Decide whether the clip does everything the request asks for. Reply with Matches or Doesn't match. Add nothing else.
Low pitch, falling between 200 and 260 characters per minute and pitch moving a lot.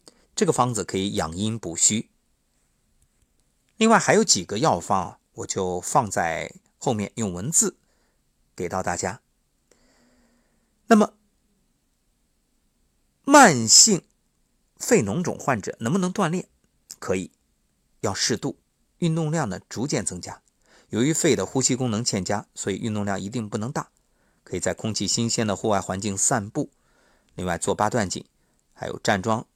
Matches